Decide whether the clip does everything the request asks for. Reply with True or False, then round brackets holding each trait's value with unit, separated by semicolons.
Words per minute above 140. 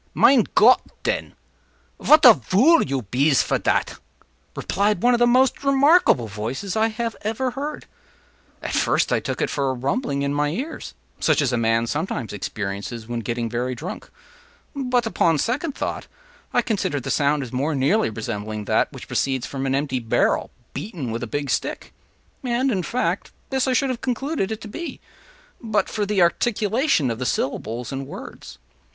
True (175 wpm)